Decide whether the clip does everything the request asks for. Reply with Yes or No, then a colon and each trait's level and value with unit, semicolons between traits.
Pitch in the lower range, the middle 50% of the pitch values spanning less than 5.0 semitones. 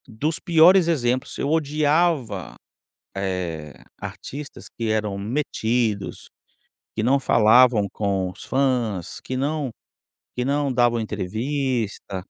No: low, 120 Hz; average, 5.3 semitones